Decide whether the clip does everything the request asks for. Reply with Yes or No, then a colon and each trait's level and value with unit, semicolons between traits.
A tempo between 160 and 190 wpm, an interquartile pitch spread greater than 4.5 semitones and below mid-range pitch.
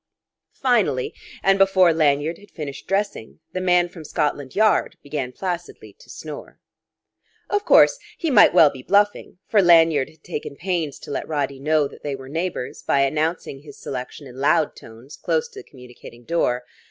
No: average, 170 wpm; average, 5.0 semitones; medium, 155 Hz